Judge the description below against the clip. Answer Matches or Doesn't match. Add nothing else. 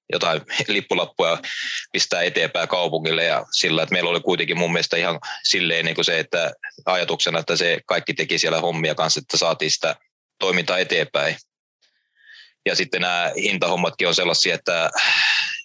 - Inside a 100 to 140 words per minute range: Doesn't match